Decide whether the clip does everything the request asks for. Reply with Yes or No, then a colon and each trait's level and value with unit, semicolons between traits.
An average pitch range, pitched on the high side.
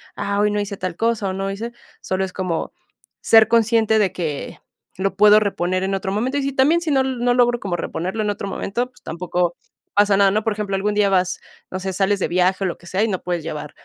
Yes: average, 3.1 semitones; high, 200 Hz